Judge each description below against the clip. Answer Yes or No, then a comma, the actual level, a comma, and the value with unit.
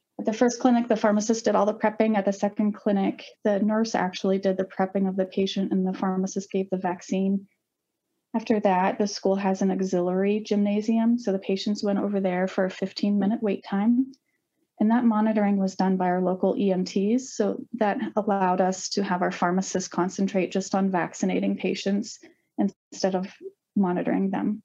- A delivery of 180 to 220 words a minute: Yes, average, 185 wpm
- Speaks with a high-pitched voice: Yes, high, 200 Hz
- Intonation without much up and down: Yes, narrow, 2.3 semitones